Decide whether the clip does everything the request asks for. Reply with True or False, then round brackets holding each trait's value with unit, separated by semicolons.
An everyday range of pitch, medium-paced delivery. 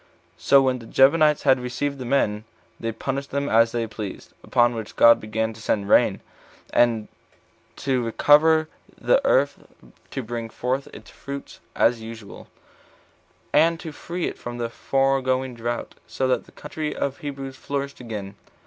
True (3.5 semitones; 160 wpm)